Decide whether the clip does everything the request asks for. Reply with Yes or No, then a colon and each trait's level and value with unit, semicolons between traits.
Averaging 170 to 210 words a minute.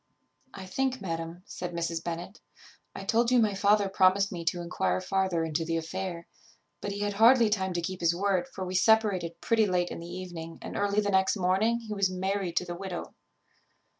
Yes: fast, 205 wpm